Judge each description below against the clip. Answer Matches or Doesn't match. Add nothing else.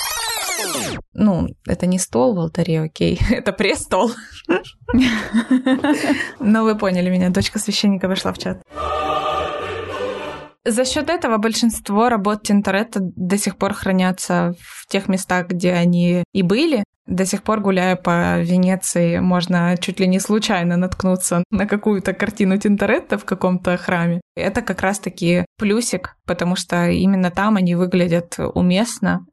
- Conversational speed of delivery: Matches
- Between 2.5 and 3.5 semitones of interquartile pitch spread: Matches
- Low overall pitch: Doesn't match